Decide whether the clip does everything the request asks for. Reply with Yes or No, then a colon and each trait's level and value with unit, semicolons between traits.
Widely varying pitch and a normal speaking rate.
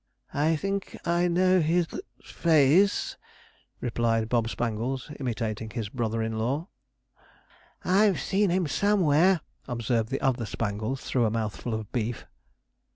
No: wide, 7.3 semitones; slow, 130 wpm